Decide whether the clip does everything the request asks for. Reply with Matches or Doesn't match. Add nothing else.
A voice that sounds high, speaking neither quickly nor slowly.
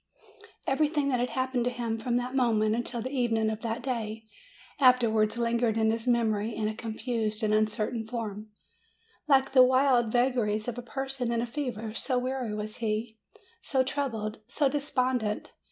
Matches